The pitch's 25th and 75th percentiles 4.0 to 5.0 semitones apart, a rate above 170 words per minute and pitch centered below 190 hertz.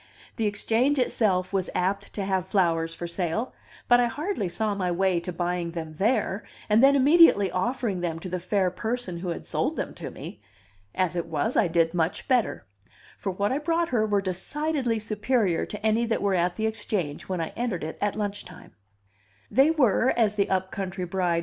No: average, 4.4 semitones; average, 180 wpm; high, 200 Hz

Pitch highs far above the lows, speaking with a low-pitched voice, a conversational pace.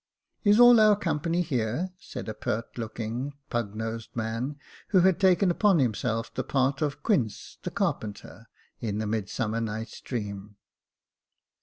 Yes: wide, 7.6 semitones; low, 120 Hz; average, 160 wpm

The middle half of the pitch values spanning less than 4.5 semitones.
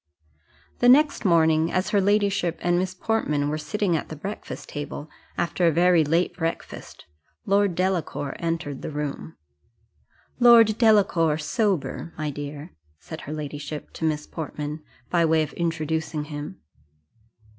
Yes: average, 3.9 semitones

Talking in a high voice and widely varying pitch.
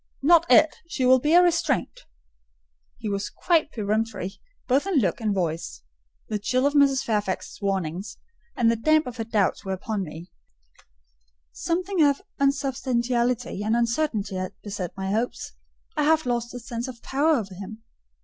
Yes: high, 235 Hz; wide, 5.7 semitones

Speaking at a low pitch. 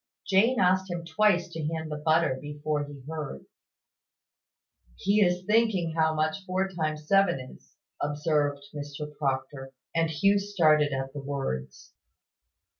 No: medium, 155 Hz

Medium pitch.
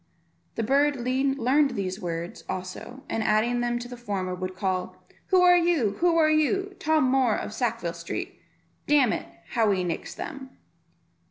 No: high, 245 Hz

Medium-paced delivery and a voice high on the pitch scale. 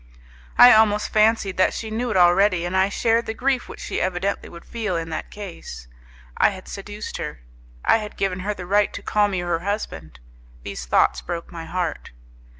Yes: average, 195 wpm; high, 195 Hz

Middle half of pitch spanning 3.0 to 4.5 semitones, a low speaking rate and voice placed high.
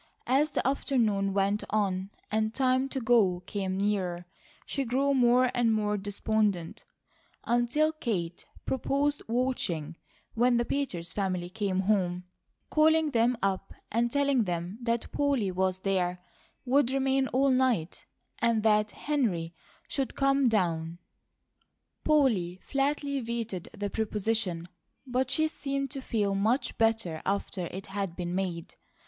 No: wide, 5.6 semitones; slow, 130 wpm; high, 220 Hz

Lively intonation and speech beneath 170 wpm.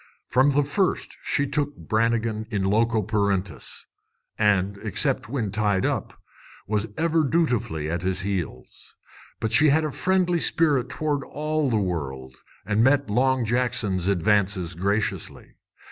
Yes: wide, 6.3 semitones; slow, 135 wpm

